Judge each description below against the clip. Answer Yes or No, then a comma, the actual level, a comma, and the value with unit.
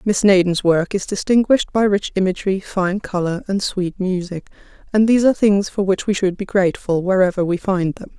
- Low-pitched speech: No, high, 190 Hz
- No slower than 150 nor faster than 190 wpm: No, average, 200 wpm